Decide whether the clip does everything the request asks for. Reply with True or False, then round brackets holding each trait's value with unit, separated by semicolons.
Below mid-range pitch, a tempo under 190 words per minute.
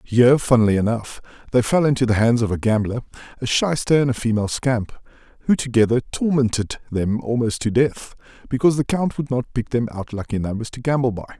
False (120 Hz; 195 wpm)